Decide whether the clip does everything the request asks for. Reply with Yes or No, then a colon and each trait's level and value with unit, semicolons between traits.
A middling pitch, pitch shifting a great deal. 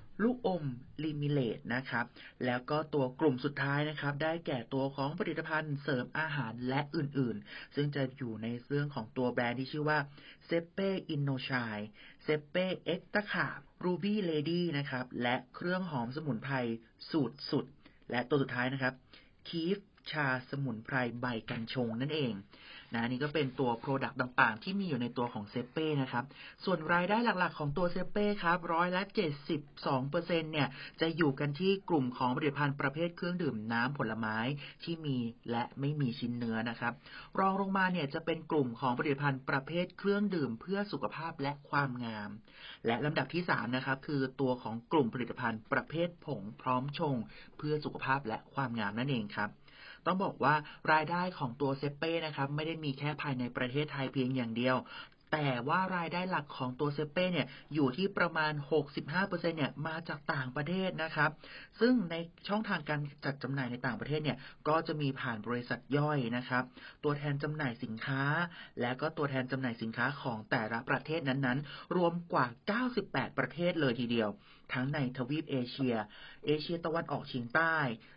No: medium, 145 Hz; average, 4.2 semitones